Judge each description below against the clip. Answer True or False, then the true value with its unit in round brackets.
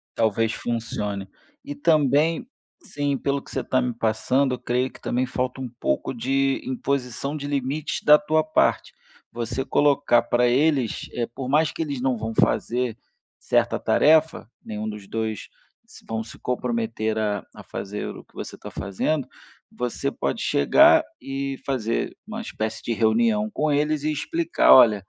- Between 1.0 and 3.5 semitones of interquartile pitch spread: False (4.5 semitones)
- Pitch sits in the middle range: False (130 Hz)